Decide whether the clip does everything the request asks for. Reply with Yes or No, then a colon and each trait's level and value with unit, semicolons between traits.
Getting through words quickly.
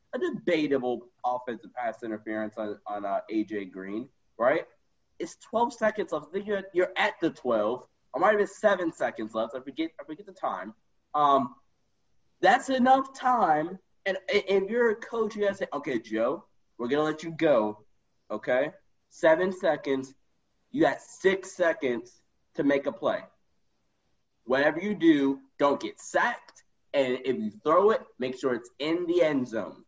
No: average, 170 wpm